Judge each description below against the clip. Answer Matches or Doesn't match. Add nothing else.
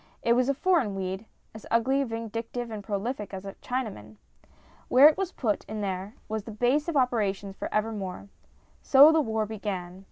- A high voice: Matches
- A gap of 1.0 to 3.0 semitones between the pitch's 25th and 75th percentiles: Doesn't match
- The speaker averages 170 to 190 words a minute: Matches